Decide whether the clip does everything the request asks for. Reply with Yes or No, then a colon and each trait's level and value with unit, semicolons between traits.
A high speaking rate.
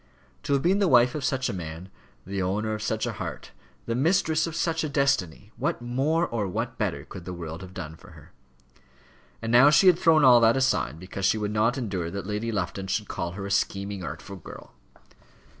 Yes: fast, 215 wpm